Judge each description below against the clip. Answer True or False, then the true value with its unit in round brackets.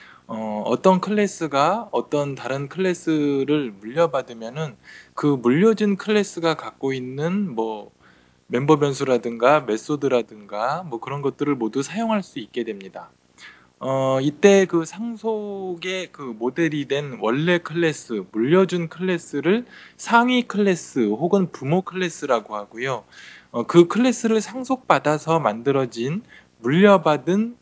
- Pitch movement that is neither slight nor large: False (7.0 semitones)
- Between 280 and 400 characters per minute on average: False (270 characters per minute)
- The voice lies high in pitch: False (155 Hz)